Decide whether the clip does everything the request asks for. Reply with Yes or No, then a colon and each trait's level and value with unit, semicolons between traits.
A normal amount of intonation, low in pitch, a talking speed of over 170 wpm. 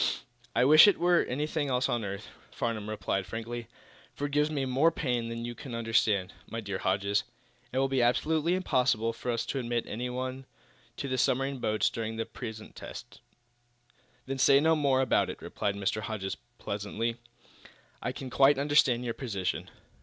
Yes: average, 3.4 semitones; low, 125 Hz; average, 180 wpm